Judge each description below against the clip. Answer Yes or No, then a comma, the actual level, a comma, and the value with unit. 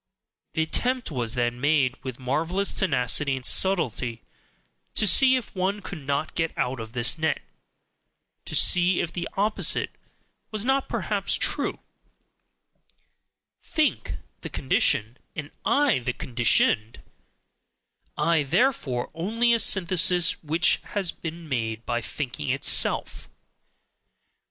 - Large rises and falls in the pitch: Yes, wide, 7.2 semitones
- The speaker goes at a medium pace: No, slow, 120 wpm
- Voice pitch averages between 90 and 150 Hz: No, medium, 160 Hz